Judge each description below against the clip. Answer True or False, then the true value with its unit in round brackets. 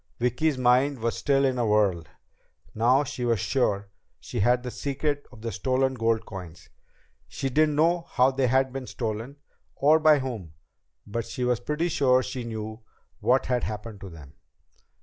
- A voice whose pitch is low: True (125 Hz)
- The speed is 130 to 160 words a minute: False (170 wpm)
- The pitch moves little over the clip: False (3.6 semitones)